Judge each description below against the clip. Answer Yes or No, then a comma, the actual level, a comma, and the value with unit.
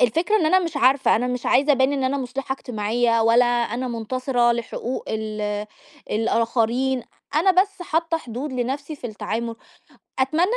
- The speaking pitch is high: Yes, very high, 250 Hz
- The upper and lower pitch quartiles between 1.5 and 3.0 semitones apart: No, average, 3.4 semitones